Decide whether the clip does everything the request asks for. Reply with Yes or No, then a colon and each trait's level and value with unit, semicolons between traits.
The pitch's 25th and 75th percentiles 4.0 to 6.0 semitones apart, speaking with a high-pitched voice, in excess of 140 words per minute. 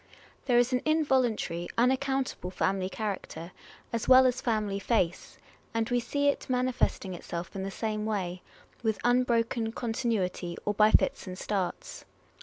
Yes: average, 4.6 semitones; high, 225 Hz; average, 150 wpm